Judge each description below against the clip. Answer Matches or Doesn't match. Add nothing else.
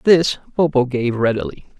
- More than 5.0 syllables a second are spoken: Doesn't match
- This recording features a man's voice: Matches